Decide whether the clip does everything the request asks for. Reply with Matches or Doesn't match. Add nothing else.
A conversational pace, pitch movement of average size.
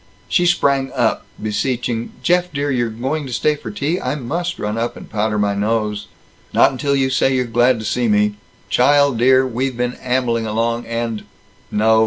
Matches